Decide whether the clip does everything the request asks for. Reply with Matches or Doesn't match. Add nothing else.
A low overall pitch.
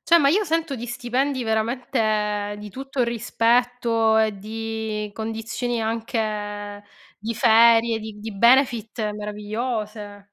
Doesn't match